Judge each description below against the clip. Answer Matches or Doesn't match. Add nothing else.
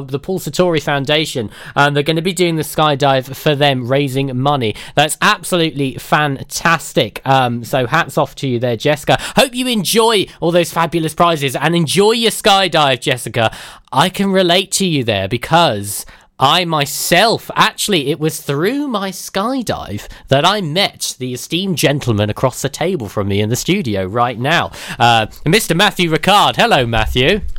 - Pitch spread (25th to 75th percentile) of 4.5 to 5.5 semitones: Matches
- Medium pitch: Matches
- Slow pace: Doesn't match